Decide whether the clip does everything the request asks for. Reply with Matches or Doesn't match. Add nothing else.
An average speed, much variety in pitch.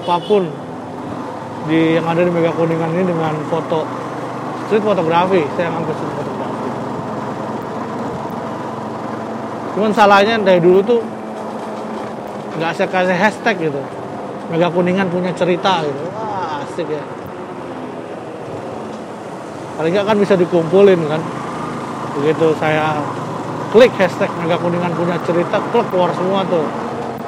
Doesn't match